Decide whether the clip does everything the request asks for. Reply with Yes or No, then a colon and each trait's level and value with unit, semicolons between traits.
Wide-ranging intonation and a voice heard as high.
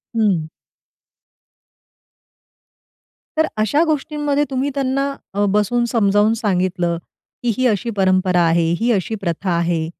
Yes: wide, 5.8 semitones; high, 210 Hz